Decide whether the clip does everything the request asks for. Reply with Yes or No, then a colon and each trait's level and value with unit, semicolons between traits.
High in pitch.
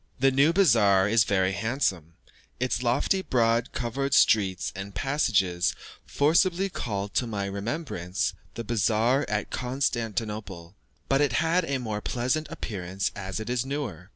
No: low, 115 Hz